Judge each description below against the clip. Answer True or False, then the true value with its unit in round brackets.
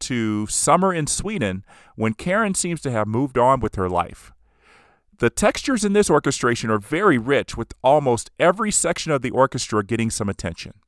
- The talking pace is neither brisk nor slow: True (175 wpm)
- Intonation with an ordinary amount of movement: False (6.8 semitones)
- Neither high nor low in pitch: False (120 Hz)